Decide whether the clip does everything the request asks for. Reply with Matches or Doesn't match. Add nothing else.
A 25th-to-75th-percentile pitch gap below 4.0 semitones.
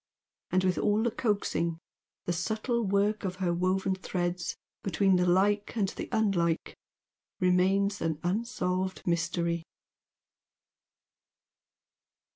Matches